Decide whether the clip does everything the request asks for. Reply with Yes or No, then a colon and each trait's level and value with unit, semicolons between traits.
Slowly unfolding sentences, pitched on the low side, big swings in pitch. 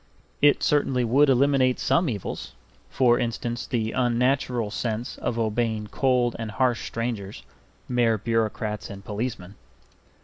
No: slow, 125 wpm; low, 120 Hz; narrow, 2.5 semitones